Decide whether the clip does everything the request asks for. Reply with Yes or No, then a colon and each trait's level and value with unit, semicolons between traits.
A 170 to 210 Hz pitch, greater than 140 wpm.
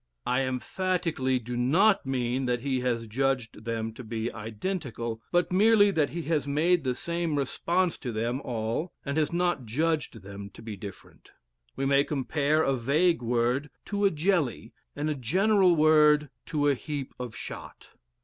No: medium, 140 Hz; average, 170 wpm